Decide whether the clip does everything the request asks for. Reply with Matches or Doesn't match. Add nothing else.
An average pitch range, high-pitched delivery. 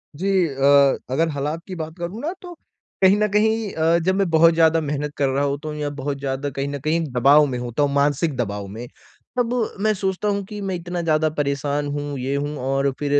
Doesn't match